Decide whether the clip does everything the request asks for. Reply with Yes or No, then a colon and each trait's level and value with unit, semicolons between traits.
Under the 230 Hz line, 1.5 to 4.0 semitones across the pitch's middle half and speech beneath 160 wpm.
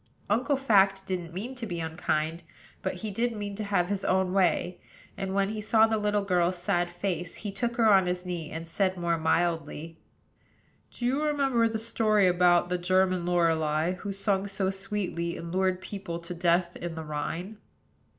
No: medium, 185 Hz; average, 3.2 semitones; average, 185 wpm